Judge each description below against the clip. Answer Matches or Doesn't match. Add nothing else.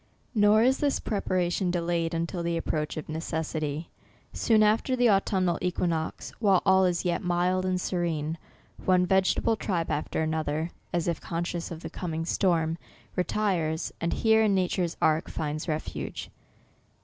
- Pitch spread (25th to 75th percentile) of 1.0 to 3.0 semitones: Matches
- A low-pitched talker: Doesn't match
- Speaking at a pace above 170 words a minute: Doesn't match